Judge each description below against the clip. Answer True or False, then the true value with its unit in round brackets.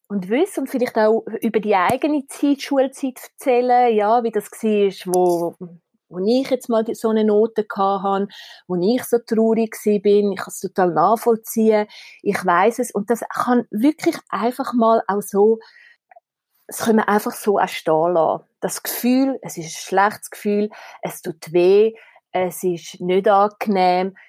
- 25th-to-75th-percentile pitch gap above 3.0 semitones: True (3.8 semitones)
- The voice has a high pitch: True (215 Hz)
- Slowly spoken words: False (155 wpm)